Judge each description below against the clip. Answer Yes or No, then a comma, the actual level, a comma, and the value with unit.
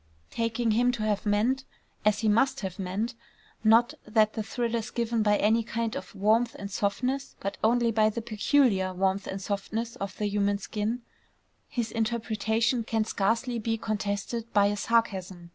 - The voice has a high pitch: Yes, high, 220 Hz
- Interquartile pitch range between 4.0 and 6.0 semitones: No, narrow, 2.4 semitones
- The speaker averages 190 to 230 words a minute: No, average, 170 wpm